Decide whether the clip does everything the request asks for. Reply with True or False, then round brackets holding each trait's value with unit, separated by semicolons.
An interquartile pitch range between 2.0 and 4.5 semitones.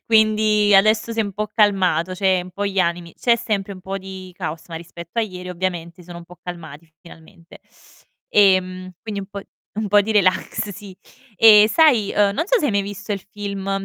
True (2.5 semitones)